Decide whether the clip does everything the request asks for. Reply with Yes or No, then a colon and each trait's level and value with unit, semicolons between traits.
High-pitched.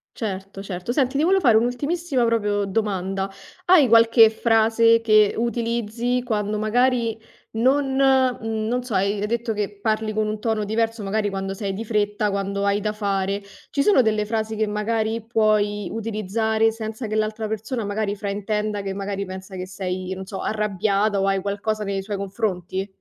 Yes: high, 215 Hz